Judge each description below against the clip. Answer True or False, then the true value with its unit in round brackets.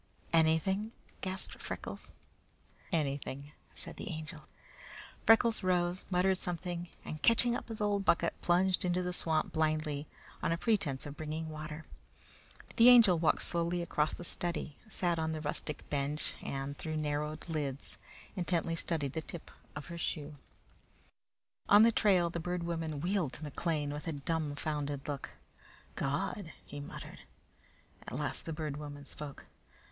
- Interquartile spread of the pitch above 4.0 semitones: False (3.1 semitones)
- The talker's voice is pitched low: False (160 Hz)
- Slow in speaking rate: False (145 wpm)